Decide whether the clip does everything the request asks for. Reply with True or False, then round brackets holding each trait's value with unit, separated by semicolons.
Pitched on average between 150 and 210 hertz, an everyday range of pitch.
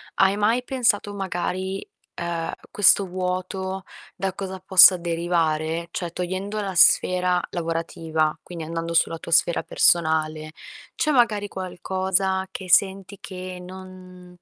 False (185 Hz; 2.1 semitones)